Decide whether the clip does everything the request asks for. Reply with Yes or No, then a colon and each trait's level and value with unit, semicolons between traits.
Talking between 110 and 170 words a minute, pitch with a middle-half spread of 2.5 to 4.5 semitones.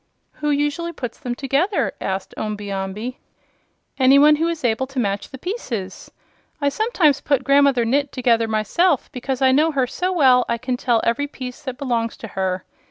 No: average, 180 wpm; average, 3.9 semitones